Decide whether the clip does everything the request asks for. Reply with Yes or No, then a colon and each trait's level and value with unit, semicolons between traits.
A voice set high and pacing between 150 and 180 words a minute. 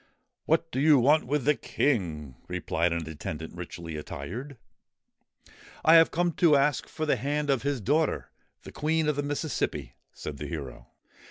No: low, 135 Hz; average, 170 wpm